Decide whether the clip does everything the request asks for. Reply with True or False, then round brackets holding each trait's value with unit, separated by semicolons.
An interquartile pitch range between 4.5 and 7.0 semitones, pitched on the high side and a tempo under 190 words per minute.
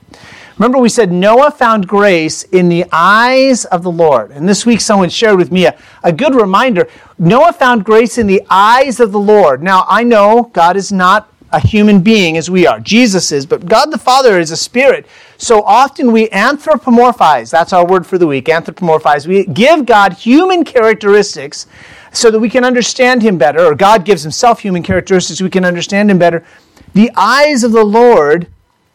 False (4.9 semitones; 210 Hz; 195 wpm)